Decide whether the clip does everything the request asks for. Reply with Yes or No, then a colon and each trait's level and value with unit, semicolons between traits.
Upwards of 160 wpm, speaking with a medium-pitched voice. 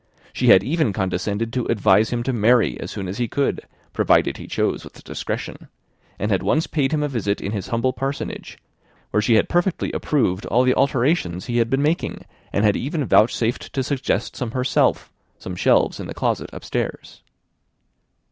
No: average, 185 wpm; low, 120 Hz